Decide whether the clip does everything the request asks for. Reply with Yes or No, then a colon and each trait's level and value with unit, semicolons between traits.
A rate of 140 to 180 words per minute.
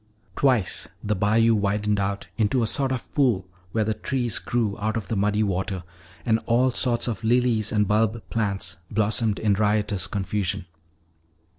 Yes: average, 160 wpm